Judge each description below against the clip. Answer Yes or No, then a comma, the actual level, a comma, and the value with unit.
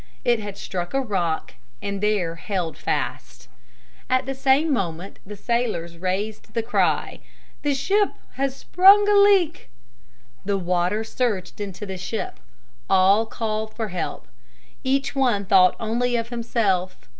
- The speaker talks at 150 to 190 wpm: No, average, 140 wpm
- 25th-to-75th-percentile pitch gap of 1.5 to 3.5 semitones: No, wide, 5.5 semitones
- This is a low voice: No, high, 215 Hz